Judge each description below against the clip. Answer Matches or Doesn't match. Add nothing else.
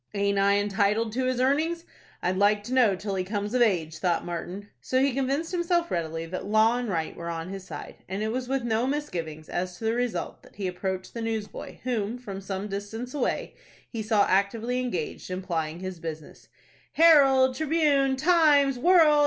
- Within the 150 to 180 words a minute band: Doesn't match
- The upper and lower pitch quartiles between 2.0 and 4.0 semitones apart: Doesn't match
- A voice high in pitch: Matches